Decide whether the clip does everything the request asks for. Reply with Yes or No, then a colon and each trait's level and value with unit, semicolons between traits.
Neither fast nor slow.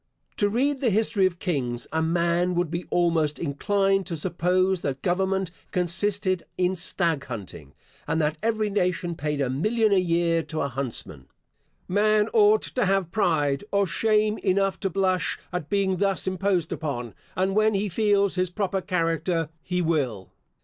Yes: average, 165 wpm